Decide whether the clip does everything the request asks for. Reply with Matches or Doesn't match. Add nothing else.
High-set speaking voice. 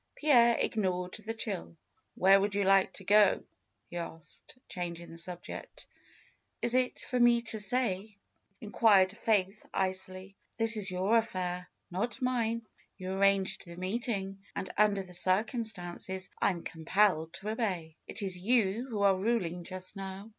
Matches